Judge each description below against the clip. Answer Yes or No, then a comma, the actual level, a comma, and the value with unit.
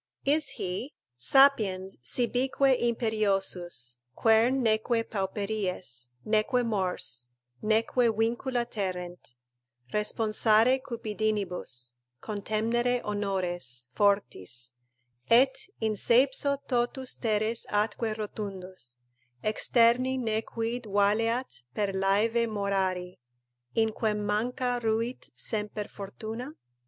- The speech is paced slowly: Yes, slow, 85 wpm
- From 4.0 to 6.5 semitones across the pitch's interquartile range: No, average, 3.5 semitones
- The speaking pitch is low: No, high, 215 Hz